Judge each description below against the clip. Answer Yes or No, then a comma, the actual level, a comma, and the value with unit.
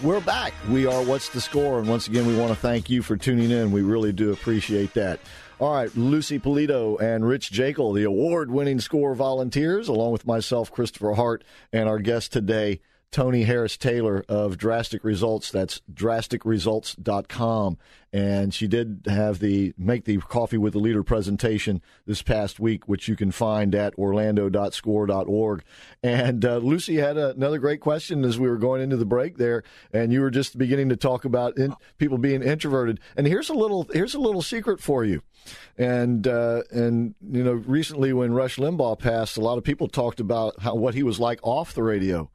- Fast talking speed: No, average, 190 wpm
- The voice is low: Yes, low, 115 Hz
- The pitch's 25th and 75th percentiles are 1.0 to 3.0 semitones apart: No, average, 3.5 semitones